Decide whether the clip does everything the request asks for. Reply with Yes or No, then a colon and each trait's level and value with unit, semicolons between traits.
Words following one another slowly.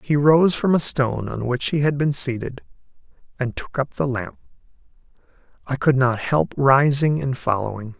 No: average, 175 wpm